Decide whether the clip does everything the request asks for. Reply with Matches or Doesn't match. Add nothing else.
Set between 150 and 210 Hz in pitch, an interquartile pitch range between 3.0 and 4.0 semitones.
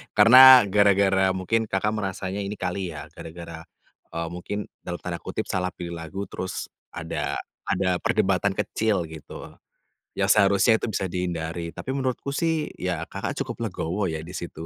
Doesn't match